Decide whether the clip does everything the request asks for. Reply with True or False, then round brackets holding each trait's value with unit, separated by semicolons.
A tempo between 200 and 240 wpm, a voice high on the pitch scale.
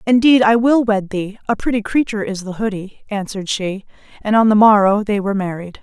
True (205 wpm; 210 Hz)